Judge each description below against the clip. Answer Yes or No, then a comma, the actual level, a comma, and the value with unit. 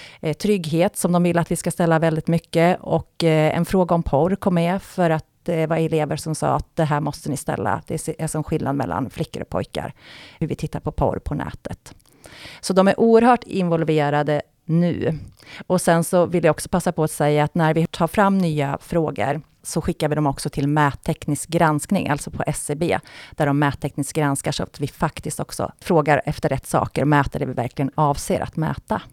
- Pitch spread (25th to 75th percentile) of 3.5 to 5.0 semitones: No, average, 2.7 semitones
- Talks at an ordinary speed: No, fast, 205 wpm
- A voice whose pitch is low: No, medium, 160 Hz